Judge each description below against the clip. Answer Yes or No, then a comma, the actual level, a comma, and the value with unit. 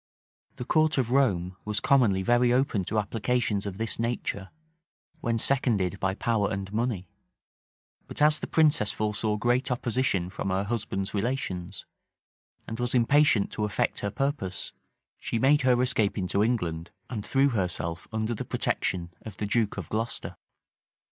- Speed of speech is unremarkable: Yes, average, 155 wpm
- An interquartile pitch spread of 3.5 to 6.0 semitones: Yes, average, 4.2 semitones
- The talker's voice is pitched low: Yes, low, 110 Hz